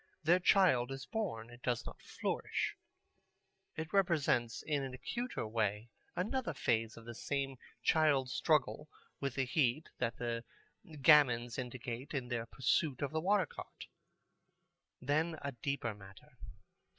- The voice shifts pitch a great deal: No, average, 4.7 semitones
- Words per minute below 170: Yes, average, 140 wpm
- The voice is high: No, low, 135 Hz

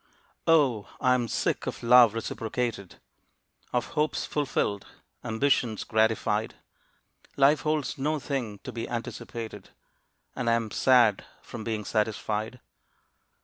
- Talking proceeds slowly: Yes, slow, 115 wpm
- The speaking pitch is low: Yes, low, 115 Hz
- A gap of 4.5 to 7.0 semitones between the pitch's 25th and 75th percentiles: No, average, 3.3 semitones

